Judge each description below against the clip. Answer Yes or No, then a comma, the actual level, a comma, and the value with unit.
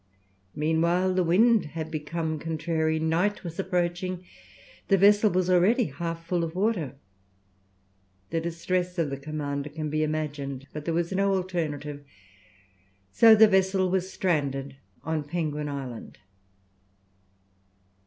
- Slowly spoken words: Yes, slow, 125 wpm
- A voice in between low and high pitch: Yes, medium, 165 Hz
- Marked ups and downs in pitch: No, average, 3.5 semitones